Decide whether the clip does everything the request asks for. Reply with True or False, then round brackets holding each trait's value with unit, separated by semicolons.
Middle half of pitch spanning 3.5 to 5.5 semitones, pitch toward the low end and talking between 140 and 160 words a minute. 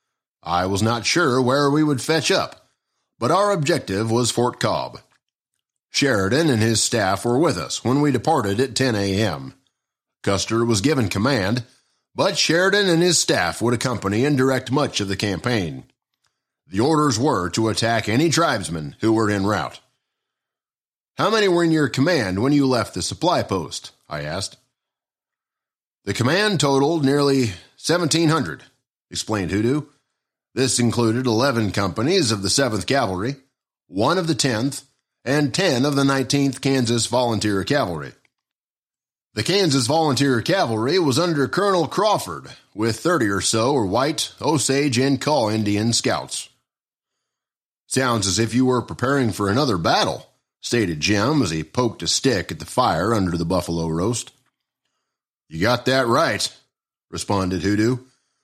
True (4.8 semitones; 125 Hz; 150 wpm)